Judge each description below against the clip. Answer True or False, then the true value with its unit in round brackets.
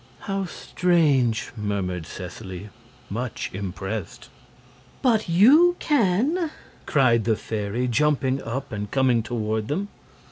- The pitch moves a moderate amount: False (9.0 semitones)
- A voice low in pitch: True (125 Hz)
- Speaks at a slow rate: True (105 wpm)